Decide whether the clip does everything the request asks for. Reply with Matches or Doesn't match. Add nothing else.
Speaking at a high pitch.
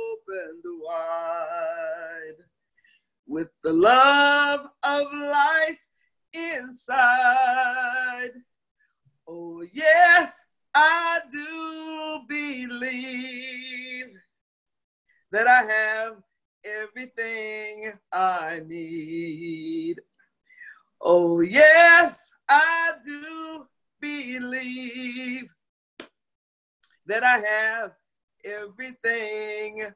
Matches